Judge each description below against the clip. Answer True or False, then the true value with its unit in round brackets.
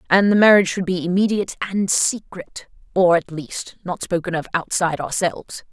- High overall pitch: False (180 Hz)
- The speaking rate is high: False (155 wpm)